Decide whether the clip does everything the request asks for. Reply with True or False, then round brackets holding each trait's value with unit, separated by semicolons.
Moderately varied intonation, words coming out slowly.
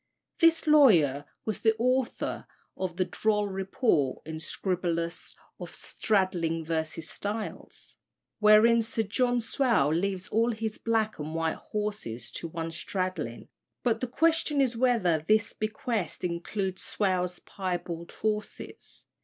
True (4.9 semitones; 125 wpm)